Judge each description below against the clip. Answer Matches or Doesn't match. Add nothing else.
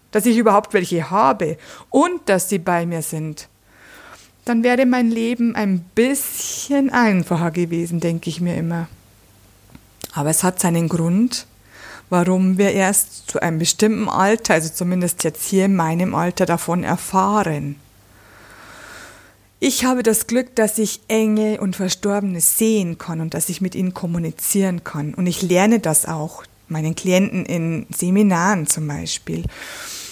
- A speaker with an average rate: Matches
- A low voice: Doesn't match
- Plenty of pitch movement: Doesn't match